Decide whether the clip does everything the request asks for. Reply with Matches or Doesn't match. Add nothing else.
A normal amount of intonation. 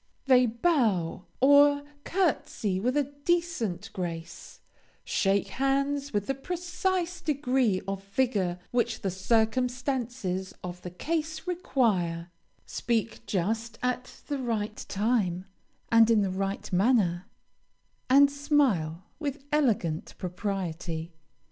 Doesn't match